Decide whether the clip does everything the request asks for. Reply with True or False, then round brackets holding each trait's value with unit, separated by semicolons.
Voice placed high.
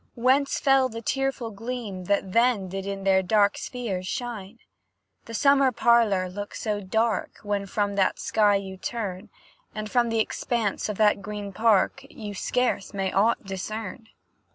True (210 Hz)